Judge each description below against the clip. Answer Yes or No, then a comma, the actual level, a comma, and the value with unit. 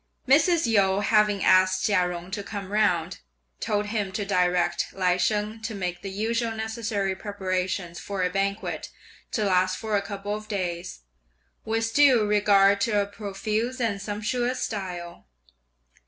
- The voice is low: No, high, 205 Hz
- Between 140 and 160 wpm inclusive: Yes, average, 150 wpm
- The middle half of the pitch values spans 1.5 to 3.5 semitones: Yes, average, 2.7 semitones